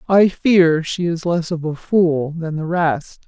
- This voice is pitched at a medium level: Yes, medium, 165 Hz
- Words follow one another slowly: No, average, 200 wpm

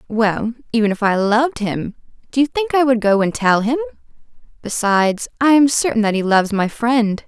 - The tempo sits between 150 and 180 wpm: No, average, 200 wpm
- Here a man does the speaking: No, female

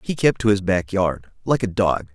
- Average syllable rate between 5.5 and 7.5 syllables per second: No, 4.8 syllables/s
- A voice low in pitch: Yes, low, 100 Hz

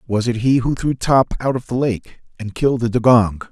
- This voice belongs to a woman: No, male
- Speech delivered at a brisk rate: Yes, fast, 240 wpm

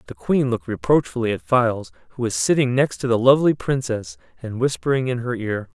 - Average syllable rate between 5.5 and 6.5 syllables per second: Yes, 5.9 syllables/s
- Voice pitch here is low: Yes, low, 120 Hz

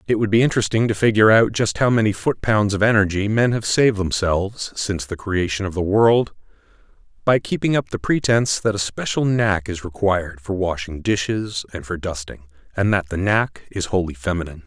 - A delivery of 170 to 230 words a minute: Yes, average, 195 wpm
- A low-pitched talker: Yes, low, 100 Hz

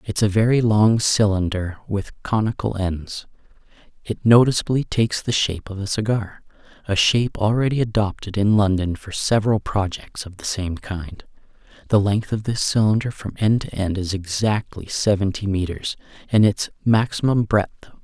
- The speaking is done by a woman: No, male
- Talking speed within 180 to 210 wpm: No, average, 170 wpm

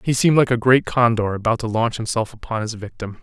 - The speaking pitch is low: Yes, low, 115 Hz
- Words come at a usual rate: No, fast, 240 wpm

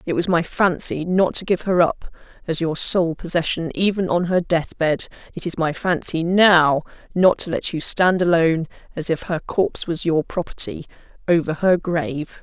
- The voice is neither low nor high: Yes, medium, 170 Hz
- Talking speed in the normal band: Yes, average, 180 wpm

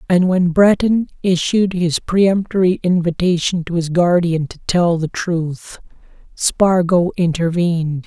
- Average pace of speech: No, slow, 120 wpm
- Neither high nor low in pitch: Yes, medium, 175 Hz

